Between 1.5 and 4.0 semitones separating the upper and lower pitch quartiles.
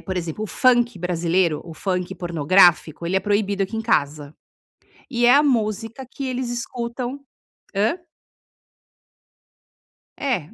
No: wide, 5.5 semitones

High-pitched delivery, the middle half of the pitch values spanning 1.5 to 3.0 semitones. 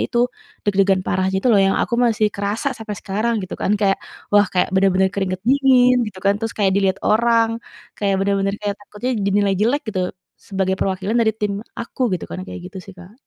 Yes: high, 200 Hz; narrow, 2.6 semitones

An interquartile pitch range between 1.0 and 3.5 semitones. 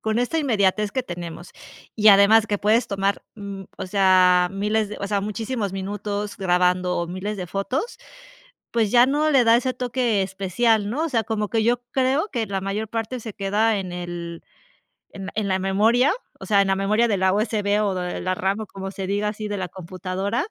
Yes: average, 2.9 semitones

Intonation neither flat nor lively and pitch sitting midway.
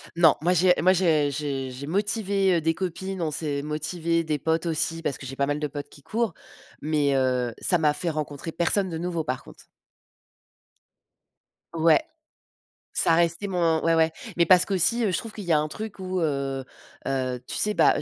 Yes: average, 3.7 semitones; medium, 165 Hz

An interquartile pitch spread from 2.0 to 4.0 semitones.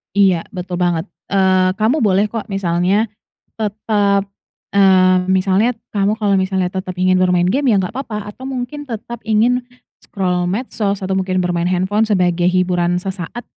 Yes: average, 2.7 semitones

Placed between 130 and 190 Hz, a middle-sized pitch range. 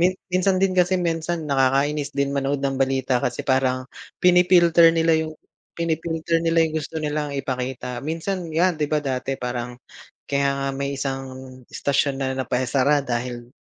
Yes: medium, 140 Hz; average, 3.8 semitones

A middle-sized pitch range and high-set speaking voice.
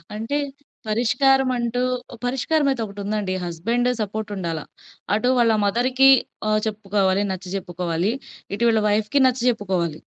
Yes: average, 4.2 semitones; high, 215 Hz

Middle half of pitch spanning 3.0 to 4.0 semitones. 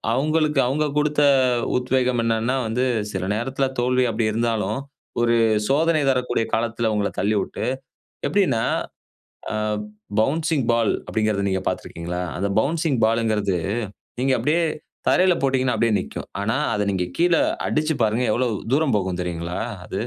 No: average, 4.5 semitones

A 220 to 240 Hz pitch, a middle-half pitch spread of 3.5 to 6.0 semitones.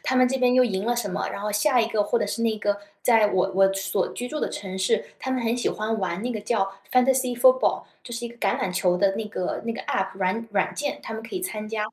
Yes: high, 225 Hz; average, 3.9 semitones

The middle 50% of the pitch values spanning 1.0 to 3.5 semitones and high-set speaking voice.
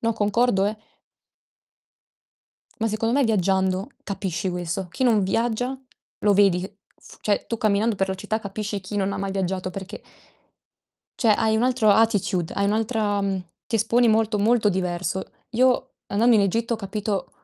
Yes: average, 2.7 semitones; high, 205 Hz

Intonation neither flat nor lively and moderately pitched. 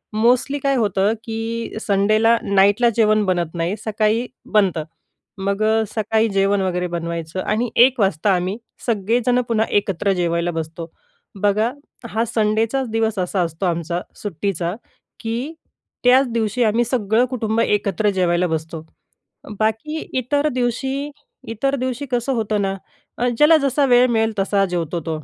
No: average, 4.0 semitones; high, 215 Hz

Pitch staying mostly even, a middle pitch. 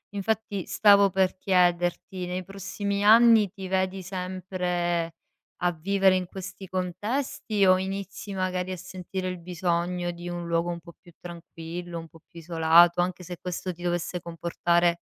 Yes: narrow, 1.8 semitones; medium, 180 Hz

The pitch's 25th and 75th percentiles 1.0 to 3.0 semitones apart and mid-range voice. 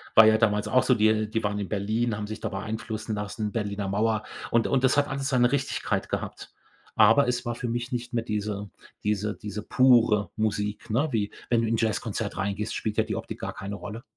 No: narrow, 2.4 semitones; low, 110 Hz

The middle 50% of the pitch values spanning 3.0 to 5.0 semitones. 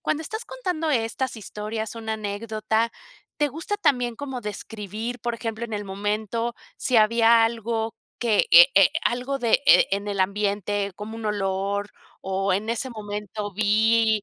No: narrow, 2.4 semitones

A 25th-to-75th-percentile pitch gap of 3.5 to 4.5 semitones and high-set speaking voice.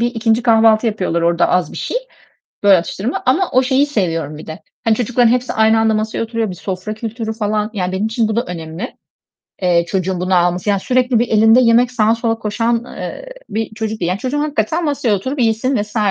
Yes: average, 4.0 semitones; high, 220 Hz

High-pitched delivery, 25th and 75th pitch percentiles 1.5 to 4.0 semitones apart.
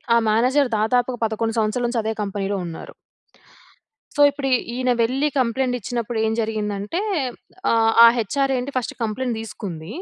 Yes: high, 230 Hz; average, 2.9 semitones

